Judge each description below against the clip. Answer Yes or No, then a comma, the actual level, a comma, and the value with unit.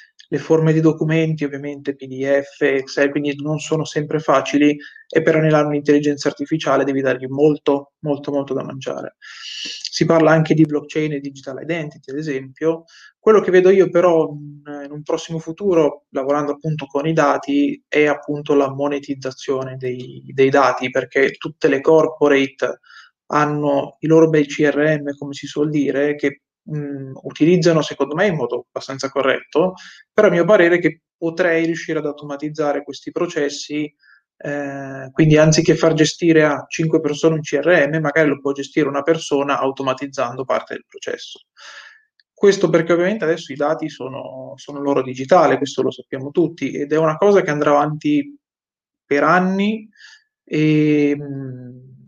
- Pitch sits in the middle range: Yes, medium, 150 Hz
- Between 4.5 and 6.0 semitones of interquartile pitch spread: No, narrow, 2.5 semitones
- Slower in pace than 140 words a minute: No, average, 155 wpm